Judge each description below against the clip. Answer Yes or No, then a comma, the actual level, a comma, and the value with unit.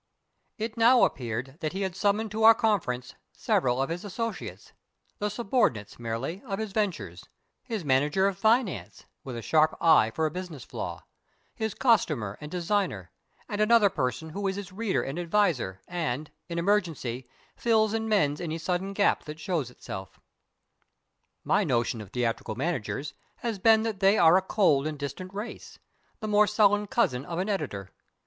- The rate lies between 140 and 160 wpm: No, average, 170 wpm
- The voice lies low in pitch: No, medium, 180 Hz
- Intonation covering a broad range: Yes, wide, 7.7 semitones